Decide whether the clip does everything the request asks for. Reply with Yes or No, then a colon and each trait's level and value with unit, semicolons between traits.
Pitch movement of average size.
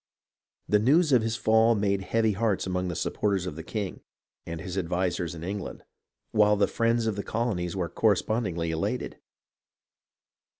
Yes: average, 3.8 semitones